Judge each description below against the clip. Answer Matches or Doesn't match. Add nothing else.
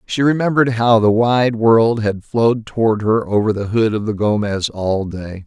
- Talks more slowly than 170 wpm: Doesn't match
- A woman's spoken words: Doesn't match